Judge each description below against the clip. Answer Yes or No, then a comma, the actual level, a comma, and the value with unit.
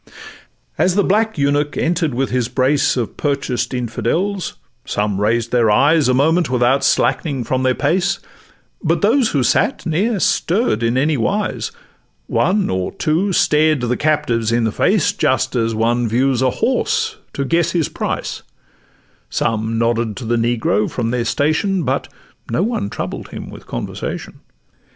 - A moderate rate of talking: Yes, average, 155 wpm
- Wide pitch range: Yes, wide, 6.3 semitones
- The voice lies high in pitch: No, low, 135 Hz